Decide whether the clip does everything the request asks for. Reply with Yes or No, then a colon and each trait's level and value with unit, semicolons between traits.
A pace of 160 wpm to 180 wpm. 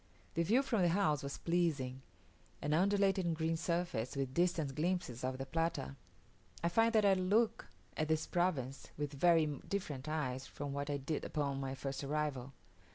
Yes: average, 170 wpm